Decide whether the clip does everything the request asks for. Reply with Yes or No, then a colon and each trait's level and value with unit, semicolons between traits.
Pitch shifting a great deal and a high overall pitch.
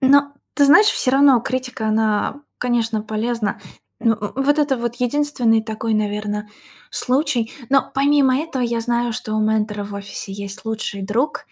No: average, 3.9 semitones; high, 235 Hz